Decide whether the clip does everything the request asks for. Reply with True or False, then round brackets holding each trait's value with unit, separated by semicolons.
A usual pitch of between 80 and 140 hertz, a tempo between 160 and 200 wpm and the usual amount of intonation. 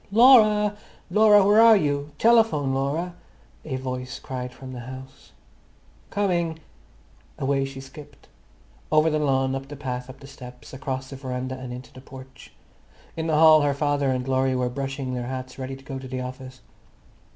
True (135 Hz; 175 wpm; 3.0 semitones)